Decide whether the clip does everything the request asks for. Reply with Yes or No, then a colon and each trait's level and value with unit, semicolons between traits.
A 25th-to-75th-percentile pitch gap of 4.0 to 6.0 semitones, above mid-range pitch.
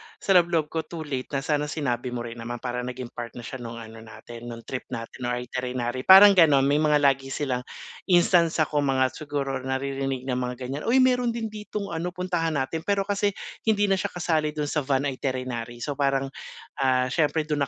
No: average, 4.5 semitones; low, 135 Hz